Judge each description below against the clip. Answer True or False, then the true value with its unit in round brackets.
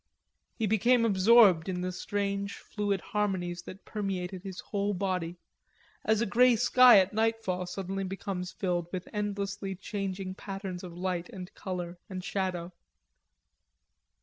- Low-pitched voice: False (195 Hz)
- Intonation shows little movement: True (2.1 semitones)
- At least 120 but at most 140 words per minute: True (135 wpm)